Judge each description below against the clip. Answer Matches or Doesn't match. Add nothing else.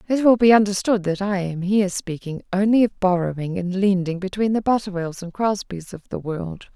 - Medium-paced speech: Matches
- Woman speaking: Matches